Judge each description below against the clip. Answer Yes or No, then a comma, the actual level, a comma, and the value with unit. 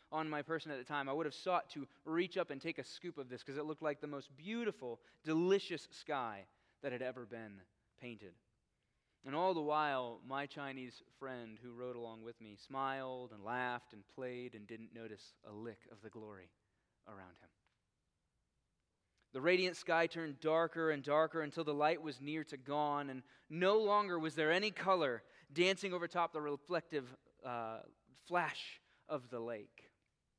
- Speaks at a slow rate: No, average, 180 wpm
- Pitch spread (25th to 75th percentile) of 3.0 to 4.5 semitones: No, wide, 5.4 semitones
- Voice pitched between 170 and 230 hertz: No, medium, 140 Hz